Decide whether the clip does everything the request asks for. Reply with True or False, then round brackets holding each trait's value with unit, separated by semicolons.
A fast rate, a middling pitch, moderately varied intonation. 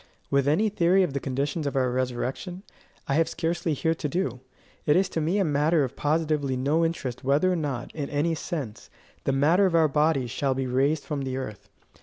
True (210 wpm; 150 Hz; 3.6 semitones)